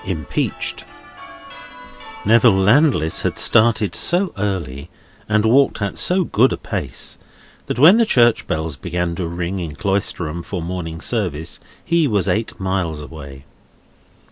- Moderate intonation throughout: No, wide, 5.9 semitones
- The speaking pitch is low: Yes, very low, 95 Hz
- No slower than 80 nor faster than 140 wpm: Yes, slow, 135 wpm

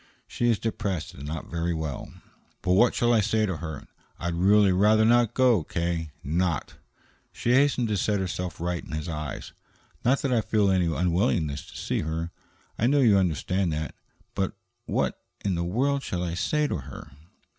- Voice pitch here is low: Yes, very low, 90 Hz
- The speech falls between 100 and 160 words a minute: No, average, 185 wpm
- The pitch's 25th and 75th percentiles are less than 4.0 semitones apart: No, average, 4.8 semitones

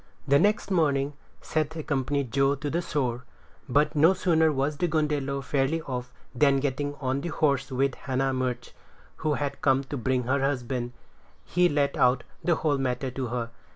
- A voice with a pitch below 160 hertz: Yes, medium, 140 Hz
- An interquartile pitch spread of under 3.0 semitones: Yes, narrow, 2.4 semitones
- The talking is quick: No, average, 175 wpm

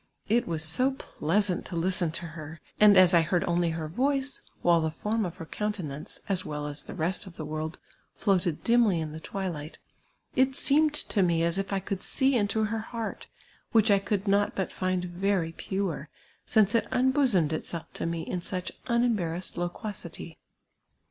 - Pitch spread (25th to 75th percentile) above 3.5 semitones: Yes, average, 4.3 semitones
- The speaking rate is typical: Yes, average, 185 wpm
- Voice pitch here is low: No, medium, 185 Hz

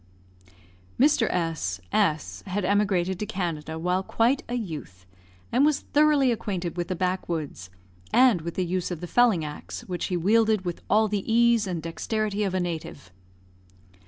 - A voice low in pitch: No, medium, 185 Hz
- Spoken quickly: No, average, 160 wpm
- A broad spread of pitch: No, average, 4.6 semitones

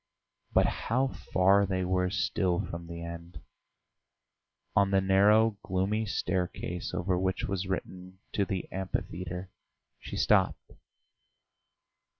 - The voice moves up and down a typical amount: No, narrow, 1.6 semitones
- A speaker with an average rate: No, slow, 115 wpm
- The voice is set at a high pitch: No, very low, 95 Hz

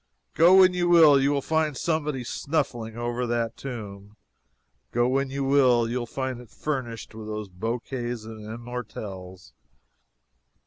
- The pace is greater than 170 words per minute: No, slow, 135 wpm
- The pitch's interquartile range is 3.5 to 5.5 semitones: Yes, average, 3.8 semitones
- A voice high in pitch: No, low, 120 Hz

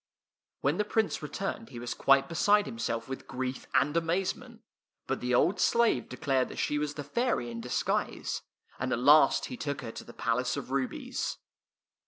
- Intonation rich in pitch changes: Yes, wide, 6.4 semitones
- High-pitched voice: No, medium, 140 Hz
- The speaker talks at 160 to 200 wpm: Yes, average, 180 wpm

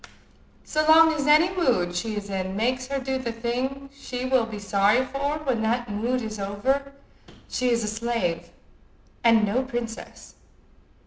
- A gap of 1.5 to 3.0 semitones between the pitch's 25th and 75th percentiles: No, average, 4.1 semitones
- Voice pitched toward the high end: Yes, high, 240 Hz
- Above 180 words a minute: No, average, 165 wpm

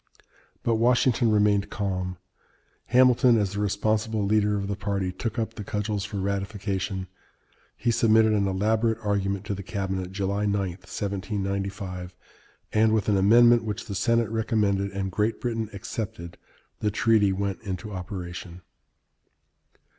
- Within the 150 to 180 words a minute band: No, average, 140 wpm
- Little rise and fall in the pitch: Yes, narrow, 2.2 semitones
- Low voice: Yes, low, 100 Hz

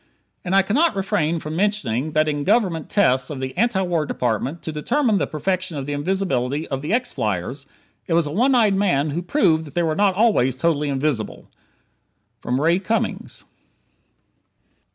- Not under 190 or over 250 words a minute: No, average, 175 wpm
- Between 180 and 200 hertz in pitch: No, medium, 165 Hz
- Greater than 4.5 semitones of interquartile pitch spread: Yes, wide, 5.5 semitones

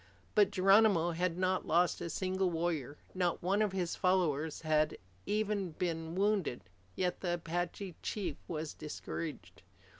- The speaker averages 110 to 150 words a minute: Yes, average, 140 wpm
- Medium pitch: Yes, medium, 175 Hz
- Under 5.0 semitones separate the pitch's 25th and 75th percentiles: Yes, narrow, 2.6 semitones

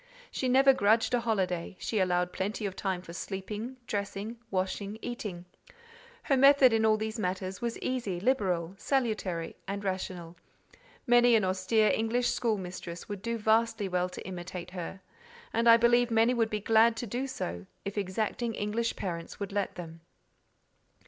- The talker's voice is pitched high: Yes, high, 210 Hz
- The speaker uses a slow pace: No, average, 160 wpm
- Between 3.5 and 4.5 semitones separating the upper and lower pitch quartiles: Yes, average, 3.9 semitones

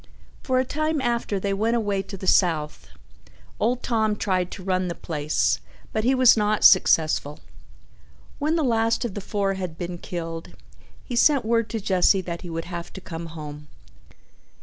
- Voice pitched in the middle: No, high, 195 Hz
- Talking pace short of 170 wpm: No, average, 175 wpm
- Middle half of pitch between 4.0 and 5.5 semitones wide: Yes, average, 5.1 semitones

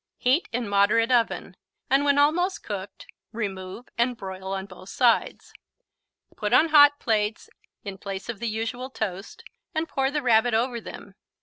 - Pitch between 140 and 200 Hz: No, high, 230 Hz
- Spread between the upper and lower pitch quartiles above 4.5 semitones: Yes, average, 4.9 semitones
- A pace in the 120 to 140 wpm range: No, average, 160 wpm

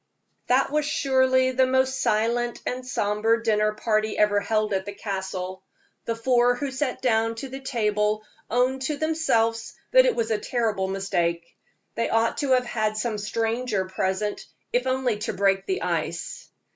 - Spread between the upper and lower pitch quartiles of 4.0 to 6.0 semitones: No, average, 3.5 semitones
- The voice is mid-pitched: No, high, 230 Hz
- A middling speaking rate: Yes, average, 165 wpm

